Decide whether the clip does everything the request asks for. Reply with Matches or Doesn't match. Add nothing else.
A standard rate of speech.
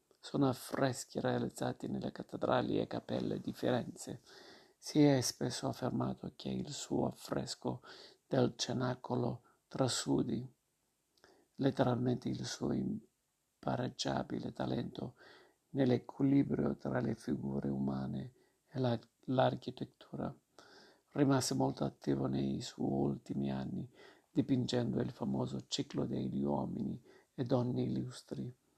Doesn't match